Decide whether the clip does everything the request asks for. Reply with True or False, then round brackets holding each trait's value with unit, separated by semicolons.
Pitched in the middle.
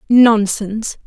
False (220 Hz)